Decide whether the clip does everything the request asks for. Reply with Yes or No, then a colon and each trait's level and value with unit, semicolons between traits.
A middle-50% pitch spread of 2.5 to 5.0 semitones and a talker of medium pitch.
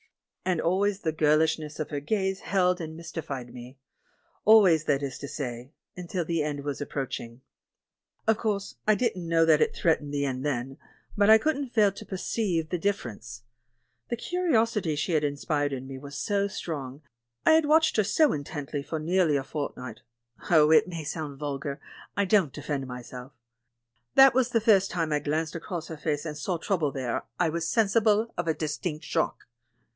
No: wide, 5.5 semitones; medium, 160 Hz